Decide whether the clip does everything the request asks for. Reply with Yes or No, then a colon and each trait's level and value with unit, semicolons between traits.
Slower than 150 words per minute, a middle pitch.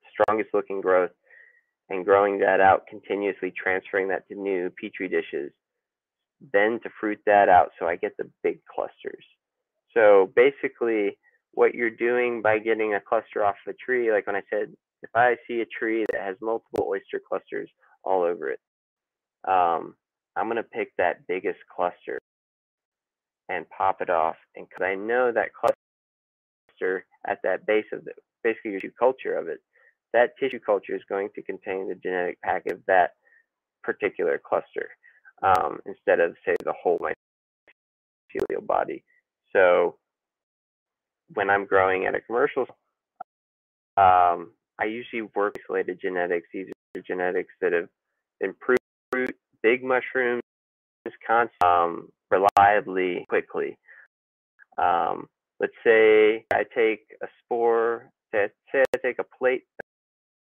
No: average, 140 wpm; very high, 400 Hz